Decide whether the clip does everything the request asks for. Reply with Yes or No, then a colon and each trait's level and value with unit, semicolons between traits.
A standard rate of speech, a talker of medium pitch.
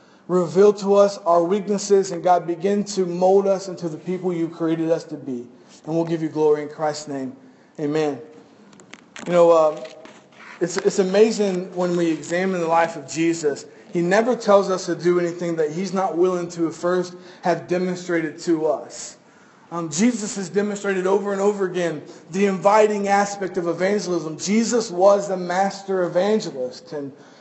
Yes: average, 170 wpm; medium, 180 Hz